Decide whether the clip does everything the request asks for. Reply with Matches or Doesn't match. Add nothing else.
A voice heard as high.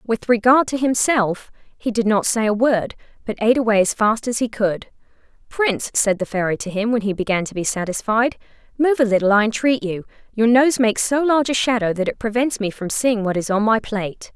Matches